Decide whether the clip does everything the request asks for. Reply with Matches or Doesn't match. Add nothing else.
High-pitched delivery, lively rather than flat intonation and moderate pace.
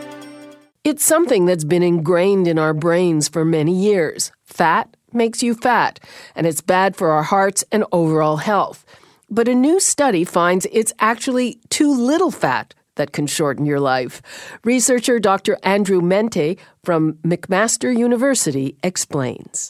Matches